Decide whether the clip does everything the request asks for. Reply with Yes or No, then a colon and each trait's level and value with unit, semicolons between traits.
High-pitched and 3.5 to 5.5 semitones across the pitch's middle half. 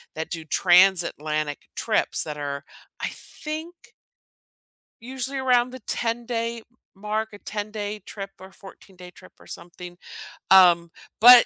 Yes: high, 200 Hz; average, 5.1 semitones